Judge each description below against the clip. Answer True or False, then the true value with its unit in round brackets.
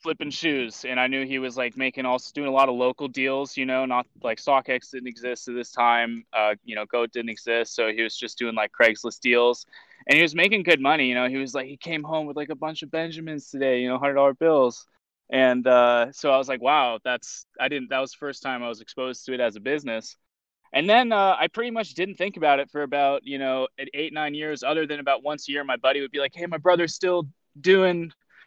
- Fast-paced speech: True (260 wpm)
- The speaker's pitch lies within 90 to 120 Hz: False (135 Hz)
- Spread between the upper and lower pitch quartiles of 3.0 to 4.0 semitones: True (3.4 semitones)